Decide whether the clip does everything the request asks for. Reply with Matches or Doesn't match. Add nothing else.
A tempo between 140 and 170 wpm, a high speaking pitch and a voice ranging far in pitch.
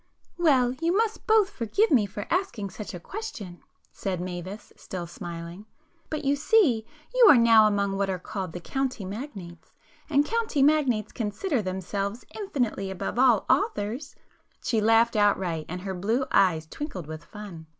Matches